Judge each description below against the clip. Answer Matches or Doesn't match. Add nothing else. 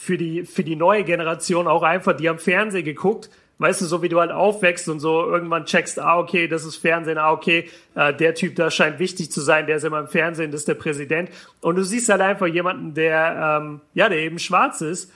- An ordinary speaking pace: Doesn't match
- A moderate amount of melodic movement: Doesn't match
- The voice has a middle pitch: Matches